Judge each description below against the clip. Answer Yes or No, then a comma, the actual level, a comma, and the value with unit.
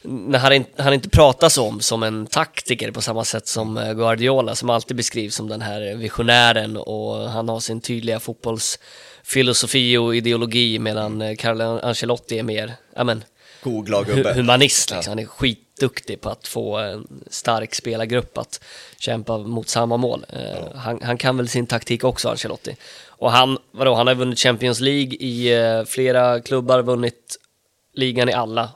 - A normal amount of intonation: No, narrow, 2.0 semitones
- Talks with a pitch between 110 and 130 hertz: Yes, low, 120 Hz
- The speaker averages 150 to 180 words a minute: Yes, average, 160 wpm